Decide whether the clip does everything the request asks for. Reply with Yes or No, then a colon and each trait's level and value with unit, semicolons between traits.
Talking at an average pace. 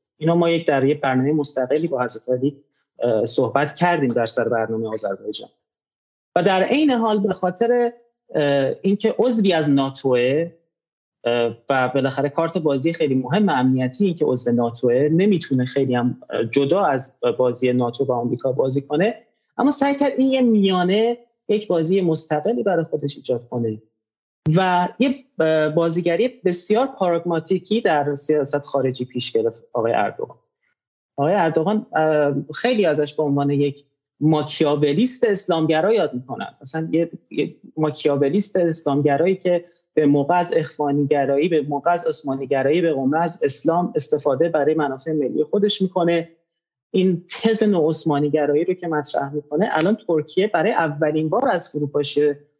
Yes: average, 140 wpm